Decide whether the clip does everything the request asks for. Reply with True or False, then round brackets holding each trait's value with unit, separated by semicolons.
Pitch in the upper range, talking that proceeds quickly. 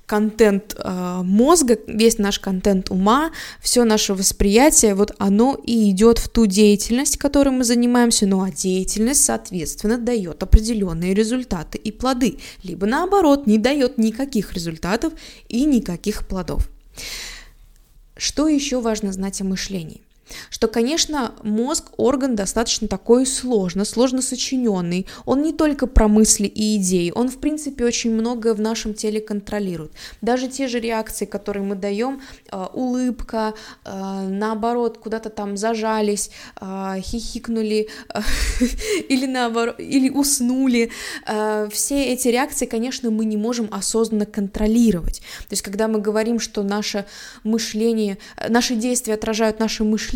False (220 Hz; 135 wpm)